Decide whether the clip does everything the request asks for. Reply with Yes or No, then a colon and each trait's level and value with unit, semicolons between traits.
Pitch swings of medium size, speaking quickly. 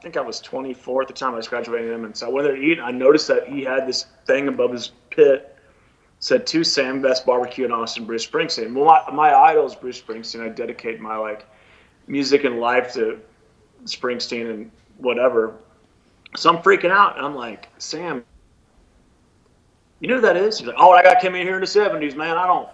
No: wide, 7.9 semitones; fast, 215 wpm